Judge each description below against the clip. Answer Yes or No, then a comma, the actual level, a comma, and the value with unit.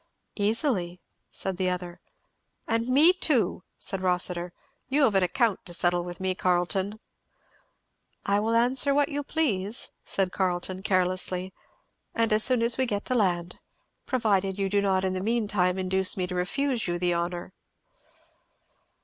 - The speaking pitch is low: No, high, 190 Hz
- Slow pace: No, average, 160 wpm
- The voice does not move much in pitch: No, average, 4.1 semitones